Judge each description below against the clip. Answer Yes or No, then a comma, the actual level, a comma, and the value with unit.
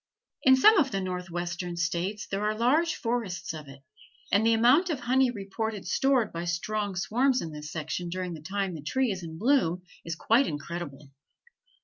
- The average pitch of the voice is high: Yes, high, 195 Hz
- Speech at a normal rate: Yes, average, 180 wpm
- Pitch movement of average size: No, wide, 5.9 semitones